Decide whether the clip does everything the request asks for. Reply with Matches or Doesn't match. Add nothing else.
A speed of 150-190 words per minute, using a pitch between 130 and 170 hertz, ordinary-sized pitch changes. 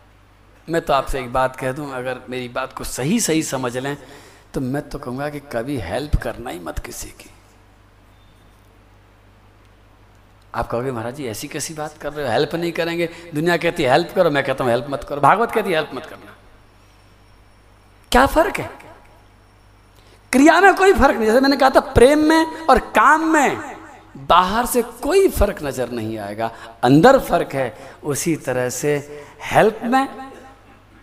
Doesn't match